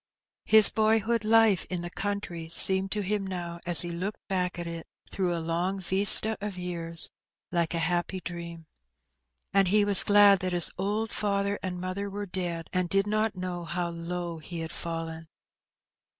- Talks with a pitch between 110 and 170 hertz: No, medium, 185 Hz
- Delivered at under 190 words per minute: Yes, average, 175 wpm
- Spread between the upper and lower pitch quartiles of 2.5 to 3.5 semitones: Yes, average, 2.9 semitones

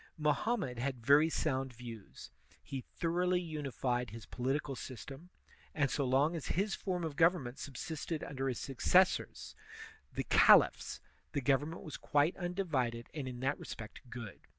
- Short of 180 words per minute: Yes, average, 150 wpm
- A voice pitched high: No, medium, 140 Hz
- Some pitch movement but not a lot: Yes, average, 4.6 semitones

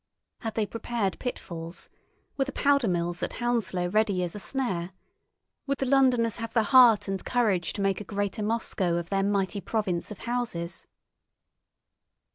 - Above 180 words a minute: No, average, 160 wpm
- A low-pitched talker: No, high, 205 Hz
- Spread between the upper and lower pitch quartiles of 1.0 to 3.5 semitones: No, average, 4.7 semitones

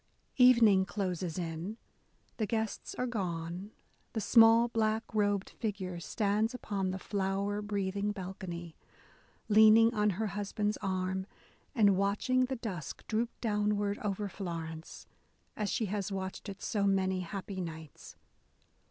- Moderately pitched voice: No, high, 200 Hz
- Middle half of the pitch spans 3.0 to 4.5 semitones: No, narrow, 2.5 semitones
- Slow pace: Yes, slow, 130 wpm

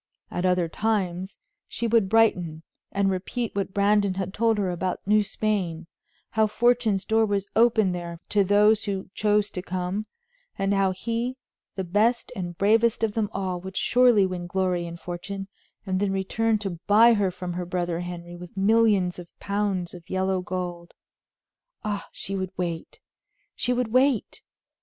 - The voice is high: Yes, high, 195 Hz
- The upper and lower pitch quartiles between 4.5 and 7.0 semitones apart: No, average, 3.1 semitones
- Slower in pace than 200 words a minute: Yes, average, 165 wpm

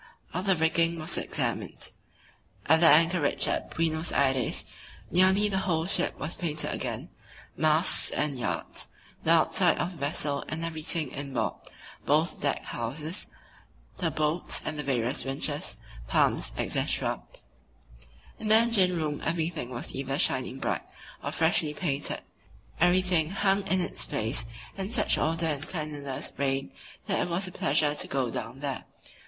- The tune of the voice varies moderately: Yes, average, 4.0 semitones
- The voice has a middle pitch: Yes, medium, 155 Hz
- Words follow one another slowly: No, average, 150 wpm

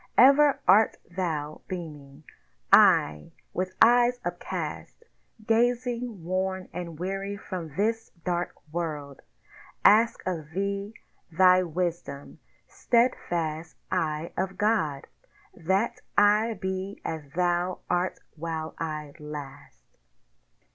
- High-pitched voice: No, medium, 180 Hz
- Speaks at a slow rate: Yes, slow, 100 wpm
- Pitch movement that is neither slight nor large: Yes, average, 4.3 semitones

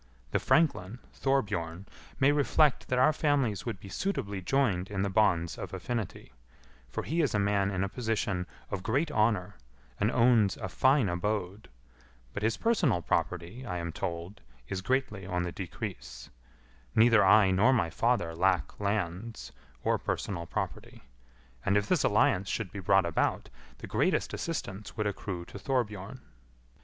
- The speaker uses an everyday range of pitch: Yes, average, 4.8 semitones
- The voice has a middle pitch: No, low, 100 Hz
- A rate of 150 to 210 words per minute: Yes, average, 155 wpm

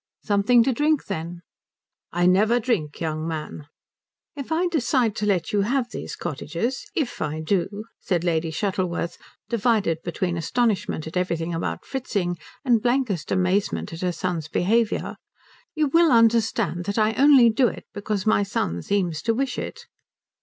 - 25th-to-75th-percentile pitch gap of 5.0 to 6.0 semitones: Yes, wide, 5.6 semitones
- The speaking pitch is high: Yes, high, 200 Hz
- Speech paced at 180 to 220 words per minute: No, average, 155 wpm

